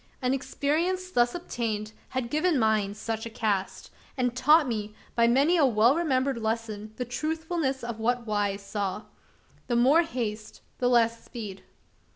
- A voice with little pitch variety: No, average, 4.3 semitones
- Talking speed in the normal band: Yes, average, 155 wpm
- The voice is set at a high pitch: Yes, high, 240 Hz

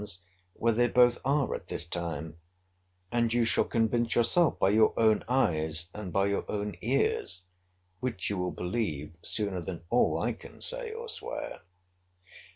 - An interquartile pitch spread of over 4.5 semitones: Yes, average, 5.3 semitones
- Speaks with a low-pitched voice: Yes, low, 105 Hz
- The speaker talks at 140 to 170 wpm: Yes, average, 160 wpm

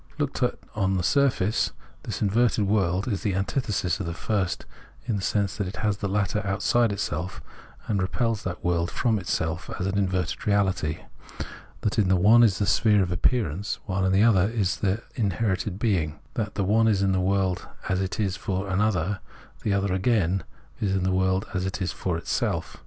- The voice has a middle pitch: No, very low, 95 Hz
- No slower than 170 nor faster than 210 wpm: Yes, average, 190 wpm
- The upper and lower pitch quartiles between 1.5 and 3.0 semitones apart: Yes, narrow, 2.4 semitones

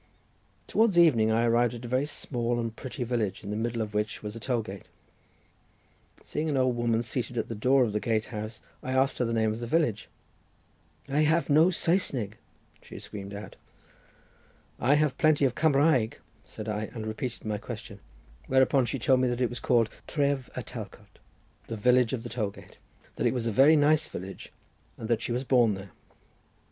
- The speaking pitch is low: Yes, low, 120 Hz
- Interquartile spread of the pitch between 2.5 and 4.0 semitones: Yes, average, 3.5 semitones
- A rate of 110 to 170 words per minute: No, average, 195 wpm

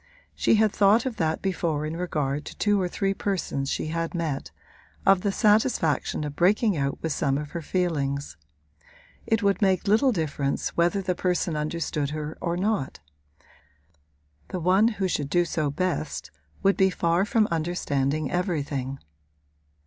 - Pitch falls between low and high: Yes, medium, 170 Hz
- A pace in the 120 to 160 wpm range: Yes, average, 155 wpm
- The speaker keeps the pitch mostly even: No, average, 4.7 semitones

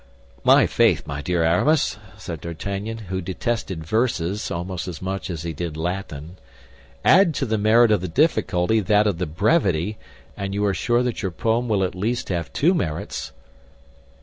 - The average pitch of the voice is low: Yes, very low, 95 Hz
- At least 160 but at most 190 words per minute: Yes, average, 175 wpm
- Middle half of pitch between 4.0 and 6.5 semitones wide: Yes, average, 4.5 semitones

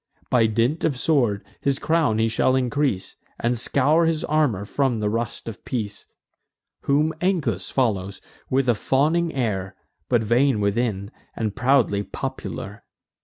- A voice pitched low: Yes, low, 120 Hz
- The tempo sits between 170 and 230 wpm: No, average, 140 wpm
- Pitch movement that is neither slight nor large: Yes, average, 4.9 semitones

